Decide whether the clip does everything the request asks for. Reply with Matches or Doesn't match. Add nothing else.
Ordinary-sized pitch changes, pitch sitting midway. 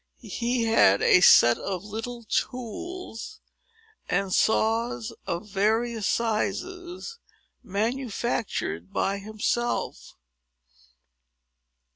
Doesn't match